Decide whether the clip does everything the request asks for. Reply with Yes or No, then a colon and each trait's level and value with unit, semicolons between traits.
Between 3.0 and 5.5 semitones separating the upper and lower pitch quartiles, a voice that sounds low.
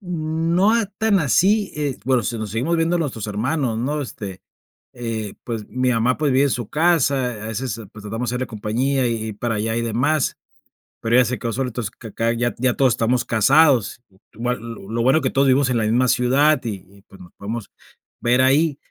Yes: average, 4.0 semitones; low, 125 Hz